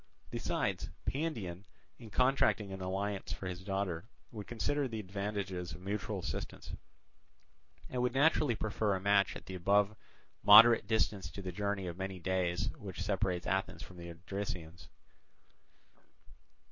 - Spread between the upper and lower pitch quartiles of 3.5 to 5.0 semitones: No, narrow, 2.6 semitones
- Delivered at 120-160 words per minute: Yes, average, 140 wpm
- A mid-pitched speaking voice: No, low, 100 Hz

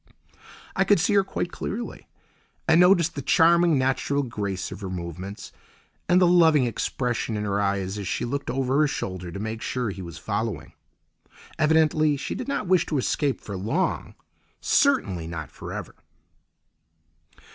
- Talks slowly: No, average, 160 wpm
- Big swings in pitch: Yes, wide, 8.9 semitones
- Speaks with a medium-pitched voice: No, low, 130 Hz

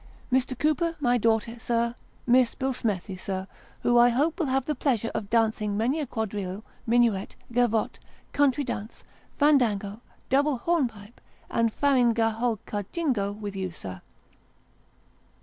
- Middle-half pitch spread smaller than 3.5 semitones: No, average, 3.9 semitones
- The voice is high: Yes, high, 235 Hz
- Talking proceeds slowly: Yes, slow, 125 wpm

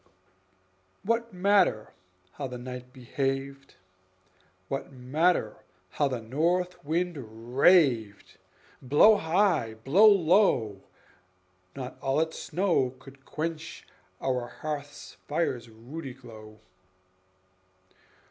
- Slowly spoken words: Yes, slow, 90 wpm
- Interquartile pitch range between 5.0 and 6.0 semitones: Yes, wide, 5.4 semitones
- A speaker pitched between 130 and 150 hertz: Yes, medium, 140 Hz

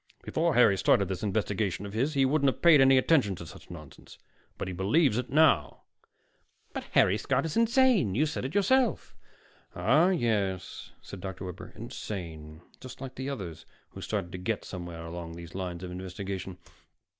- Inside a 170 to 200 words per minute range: Yes, average, 175 wpm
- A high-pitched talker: No, low, 105 Hz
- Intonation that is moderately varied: No, wide, 7.1 semitones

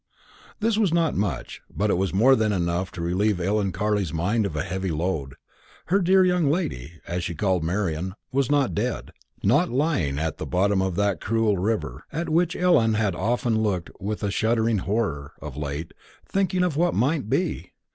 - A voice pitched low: Yes, low, 105 Hz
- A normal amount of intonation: No, wide, 7.3 semitones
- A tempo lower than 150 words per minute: No, average, 185 wpm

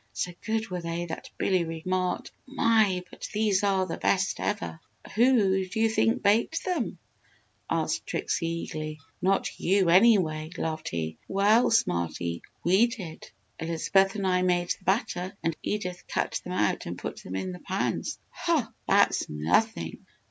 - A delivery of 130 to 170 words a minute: Yes, average, 155 wpm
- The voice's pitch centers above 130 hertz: Yes, medium, 185 Hz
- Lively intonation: No, average, 4.2 semitones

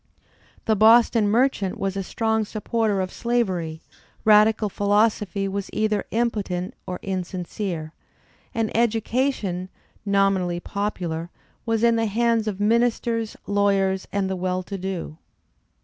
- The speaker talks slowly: Yes, slow, 120 wpm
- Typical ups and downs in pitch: Yes, average, 3.0 semitones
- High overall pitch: Yes, high, 205 Hz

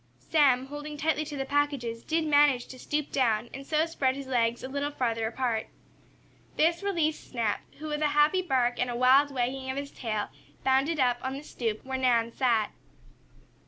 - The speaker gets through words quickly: No, average, 190 wpm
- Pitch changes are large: No, average, 3.4 semitones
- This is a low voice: No, very high, 265 Hz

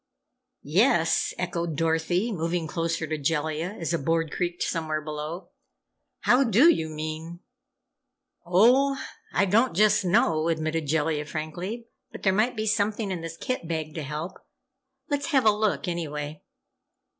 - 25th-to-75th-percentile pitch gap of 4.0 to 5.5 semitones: Yes, average, 4.7 semitones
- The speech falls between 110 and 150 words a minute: Yes, average, 145 wpm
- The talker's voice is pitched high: No, medium, 170 Hz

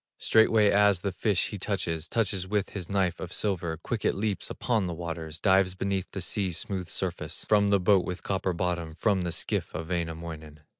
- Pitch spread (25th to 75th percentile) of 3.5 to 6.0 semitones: No, average, 3.0 semitones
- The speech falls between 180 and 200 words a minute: Yes, average, 195 wpm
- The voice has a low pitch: Yes, very low, 95 Hz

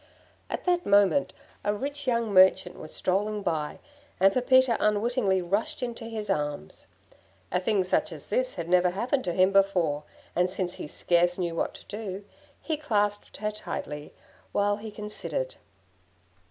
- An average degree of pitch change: Yes, average, 4.0 semitones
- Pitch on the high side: Yes, high, 200 Hz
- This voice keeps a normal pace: Yes, average, 155 wpm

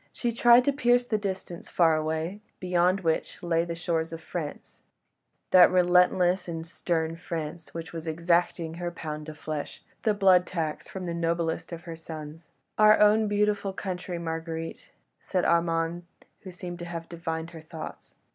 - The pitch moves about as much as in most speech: No, narrow, 2.0 semitones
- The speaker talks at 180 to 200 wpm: No, average, 165 wpm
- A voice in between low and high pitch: Yes, medium, 170 Hz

